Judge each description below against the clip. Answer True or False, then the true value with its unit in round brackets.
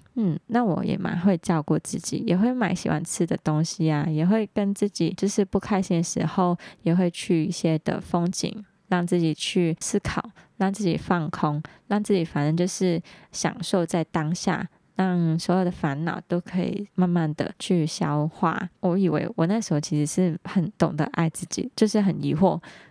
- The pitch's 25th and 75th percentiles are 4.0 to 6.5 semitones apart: False (3.1 semitones)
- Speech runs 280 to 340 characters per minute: False (260 characters per minute)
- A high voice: False (180 Hz)